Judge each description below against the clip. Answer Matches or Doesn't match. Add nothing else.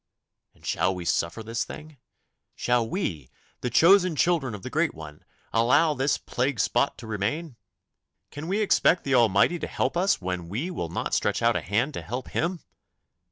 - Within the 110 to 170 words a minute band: Doesn't match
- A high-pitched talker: Doesn't match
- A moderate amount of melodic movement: Doesn't match